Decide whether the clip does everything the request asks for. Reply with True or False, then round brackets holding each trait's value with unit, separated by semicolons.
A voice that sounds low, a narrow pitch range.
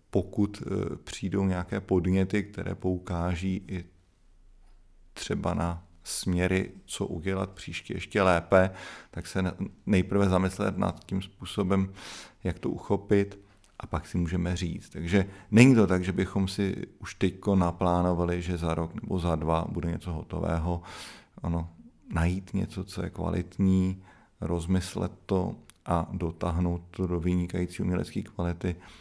True (90 Hz; 1.9 semitones)